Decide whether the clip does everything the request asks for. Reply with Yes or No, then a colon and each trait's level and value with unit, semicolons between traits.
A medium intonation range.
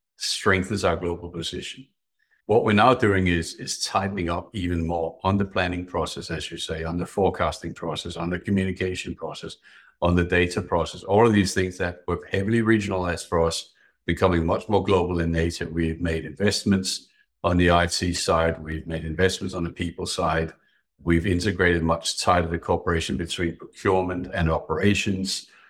No: narrow, 2.3 semitones